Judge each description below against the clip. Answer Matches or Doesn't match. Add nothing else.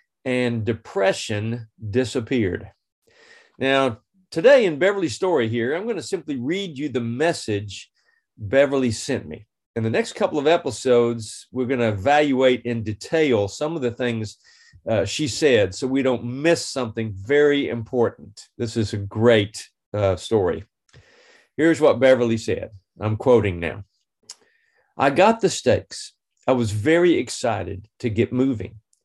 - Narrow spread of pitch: Doesn't match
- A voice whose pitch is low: Matches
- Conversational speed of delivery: Matches